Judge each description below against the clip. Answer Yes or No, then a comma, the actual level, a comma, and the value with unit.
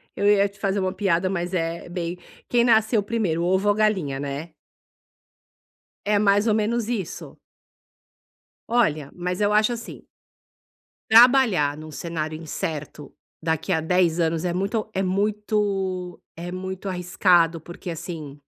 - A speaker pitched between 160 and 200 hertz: Yes, medium, 185 Hz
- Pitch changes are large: No, average, 3.9 semitones